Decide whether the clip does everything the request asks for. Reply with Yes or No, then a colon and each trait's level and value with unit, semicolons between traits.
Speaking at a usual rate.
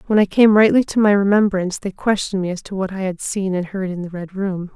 No: fast, 280 wpm